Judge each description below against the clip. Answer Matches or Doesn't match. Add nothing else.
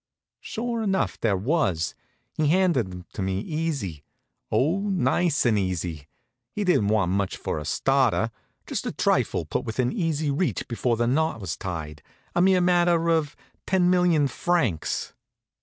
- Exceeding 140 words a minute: Matches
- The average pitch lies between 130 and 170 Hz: Matches